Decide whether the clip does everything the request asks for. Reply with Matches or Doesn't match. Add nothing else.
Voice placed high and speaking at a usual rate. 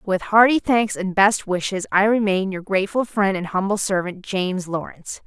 Matches